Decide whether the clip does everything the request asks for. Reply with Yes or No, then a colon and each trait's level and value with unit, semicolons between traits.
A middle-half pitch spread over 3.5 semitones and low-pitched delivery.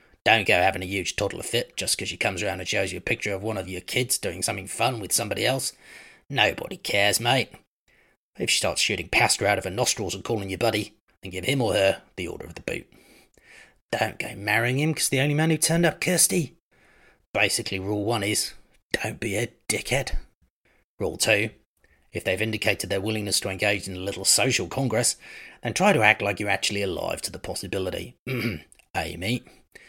Yes: average, 4.2 semitones; low, 105 Hz